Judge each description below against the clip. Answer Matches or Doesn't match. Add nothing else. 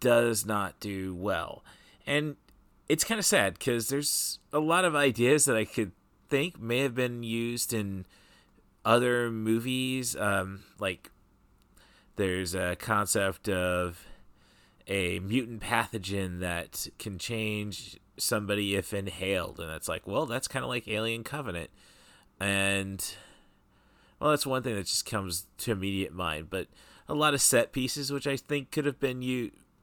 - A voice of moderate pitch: Doesn't match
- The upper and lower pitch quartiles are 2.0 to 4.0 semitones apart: Doesn't match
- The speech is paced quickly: Doesn't match